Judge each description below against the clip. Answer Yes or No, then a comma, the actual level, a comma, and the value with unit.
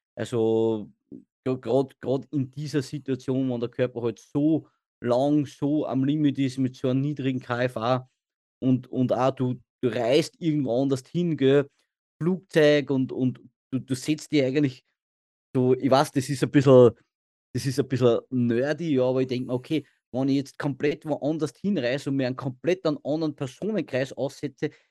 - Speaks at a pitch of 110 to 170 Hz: Yes, low, 135 Hz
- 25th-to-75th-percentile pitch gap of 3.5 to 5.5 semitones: No, narrow, 2.6 semitones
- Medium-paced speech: Yes, average, 170 wpm